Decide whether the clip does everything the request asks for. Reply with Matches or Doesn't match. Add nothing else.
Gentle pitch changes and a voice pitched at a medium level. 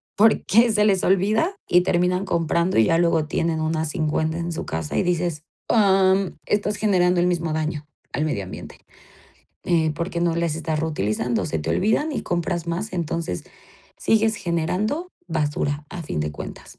Doesn't match